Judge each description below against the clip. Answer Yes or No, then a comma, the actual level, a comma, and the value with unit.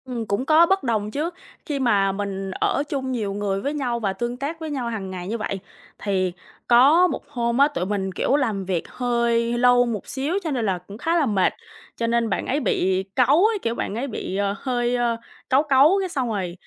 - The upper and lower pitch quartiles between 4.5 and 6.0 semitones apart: Yes, wide, 5.5 semitones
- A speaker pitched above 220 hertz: Yes, high, 235 Hz